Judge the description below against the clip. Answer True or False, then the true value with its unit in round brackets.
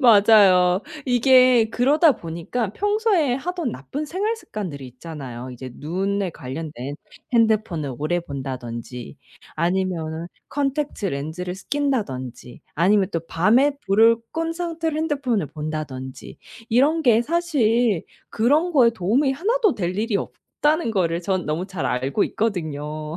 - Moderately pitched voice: False (200 Hz)